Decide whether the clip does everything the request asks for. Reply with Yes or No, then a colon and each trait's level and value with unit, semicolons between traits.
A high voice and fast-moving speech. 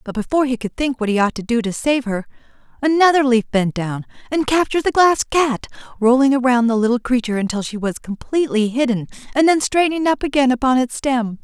Yes: very high, 250 Hz; fast, 210 wpm